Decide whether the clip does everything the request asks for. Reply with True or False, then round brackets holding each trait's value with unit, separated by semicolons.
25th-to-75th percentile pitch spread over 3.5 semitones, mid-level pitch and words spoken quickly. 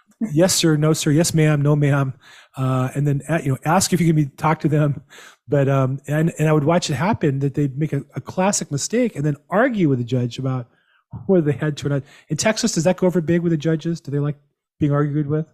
False (2.9 semitones; 155 Hz; 260 wpm)